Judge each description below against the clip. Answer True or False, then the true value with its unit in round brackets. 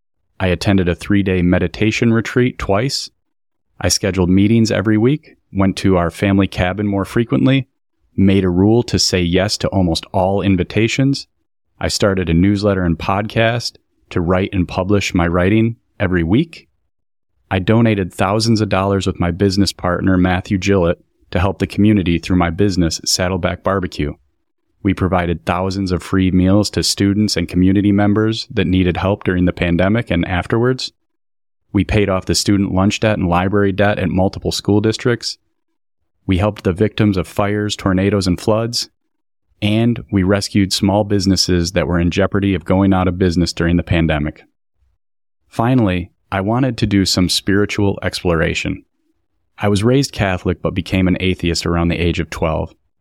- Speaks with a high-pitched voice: False (95 Hz)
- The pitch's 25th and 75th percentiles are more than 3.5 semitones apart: False (2.7 semitones)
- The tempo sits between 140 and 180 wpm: True (165 wpm)